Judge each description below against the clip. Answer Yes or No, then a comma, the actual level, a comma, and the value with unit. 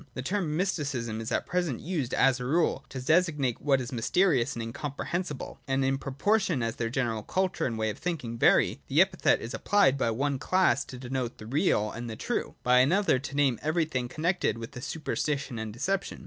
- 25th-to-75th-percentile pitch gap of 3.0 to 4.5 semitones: No, average, 5.3 semitones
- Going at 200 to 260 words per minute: Yes, fast, 205 wpm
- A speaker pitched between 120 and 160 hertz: Yes, low, 135 Hz